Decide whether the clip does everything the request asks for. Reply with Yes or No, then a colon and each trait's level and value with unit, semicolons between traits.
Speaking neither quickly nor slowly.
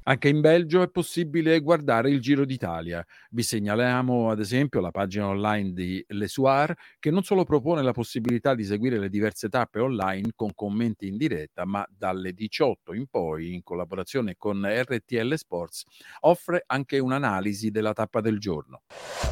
Yes: average, 160 wpm